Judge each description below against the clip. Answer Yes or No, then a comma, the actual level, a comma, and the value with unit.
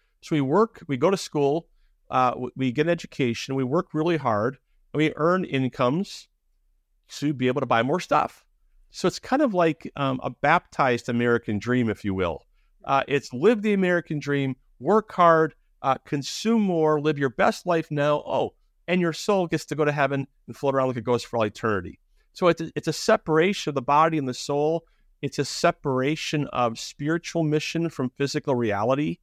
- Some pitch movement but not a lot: Yes, average, 4.5 semitones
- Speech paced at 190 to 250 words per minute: Yes, average, 195 wpm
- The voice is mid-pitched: Yes, medium, 145 Hz